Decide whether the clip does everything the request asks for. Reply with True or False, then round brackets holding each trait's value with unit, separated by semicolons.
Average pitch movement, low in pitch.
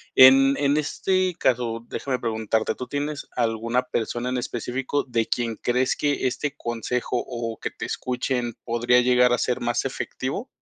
False (2.2 semitones; 125 Hz)